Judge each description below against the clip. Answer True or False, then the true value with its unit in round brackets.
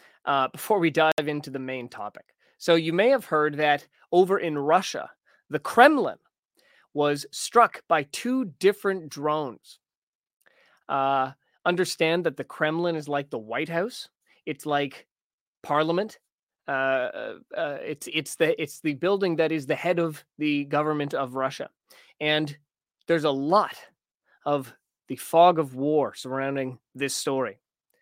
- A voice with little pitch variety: False (3.0 semitones)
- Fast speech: False (145 wpm)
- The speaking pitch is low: False (155 Hz)